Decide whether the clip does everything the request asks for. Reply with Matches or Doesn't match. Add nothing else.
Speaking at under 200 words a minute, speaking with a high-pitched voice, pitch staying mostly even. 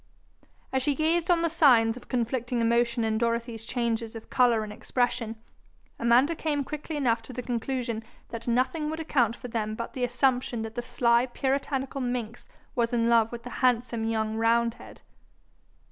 Matches